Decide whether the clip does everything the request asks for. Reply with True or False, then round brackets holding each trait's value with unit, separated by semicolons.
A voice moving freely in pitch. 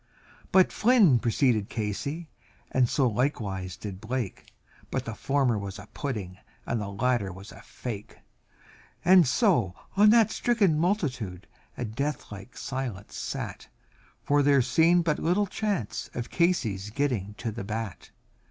True (6.9 semitones)